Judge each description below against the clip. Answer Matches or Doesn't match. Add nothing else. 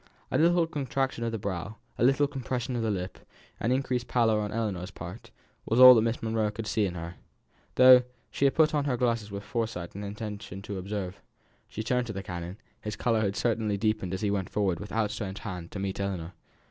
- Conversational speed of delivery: Doesn't match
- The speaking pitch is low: Matches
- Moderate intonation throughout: Matches